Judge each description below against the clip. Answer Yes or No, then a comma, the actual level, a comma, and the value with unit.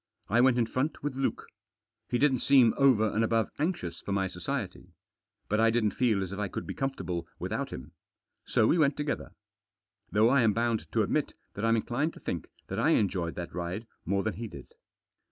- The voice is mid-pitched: No, low, 115 Hz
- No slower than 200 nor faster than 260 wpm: Yes, fast, 205 wpm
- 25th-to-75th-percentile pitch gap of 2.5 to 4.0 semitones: No, average, 4.8 semitones